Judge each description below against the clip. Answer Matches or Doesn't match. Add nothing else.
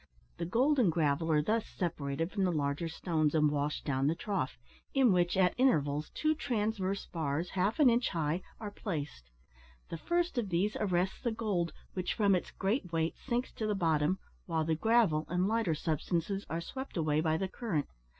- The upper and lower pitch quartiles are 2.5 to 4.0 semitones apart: Doesn't match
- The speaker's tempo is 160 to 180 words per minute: Doesn't match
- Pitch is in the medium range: Matches